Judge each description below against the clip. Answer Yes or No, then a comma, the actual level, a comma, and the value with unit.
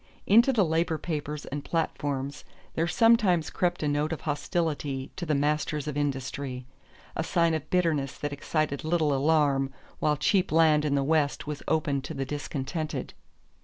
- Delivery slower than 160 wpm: No, average, 165 wpm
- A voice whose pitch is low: No, medium, 150 Hz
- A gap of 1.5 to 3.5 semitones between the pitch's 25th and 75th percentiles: Yes, narrow, 2.4 semitones